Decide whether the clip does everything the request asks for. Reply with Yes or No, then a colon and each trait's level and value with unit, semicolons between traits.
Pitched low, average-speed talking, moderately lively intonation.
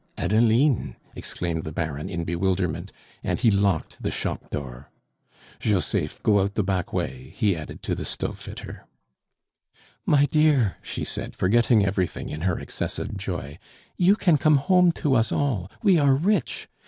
No: low, 100 Hz; average, 155 wpm; wide, 7.9 semitones